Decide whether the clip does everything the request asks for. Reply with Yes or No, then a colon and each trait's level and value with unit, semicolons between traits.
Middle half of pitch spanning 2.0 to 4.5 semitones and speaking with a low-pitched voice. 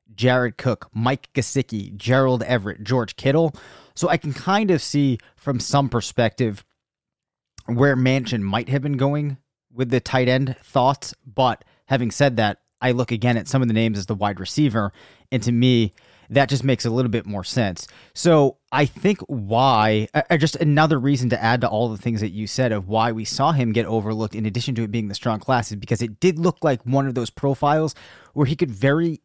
Yes: average, 3.7 semitones; low, 125 Hz